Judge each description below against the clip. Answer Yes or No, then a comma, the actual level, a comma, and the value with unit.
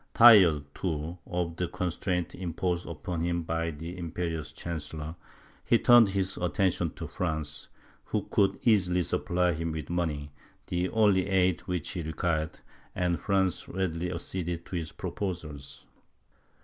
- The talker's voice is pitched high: No, very low, 85 Hz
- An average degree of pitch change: No, narrow, 2.3 semitones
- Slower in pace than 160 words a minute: Yes, slow, 135 wpm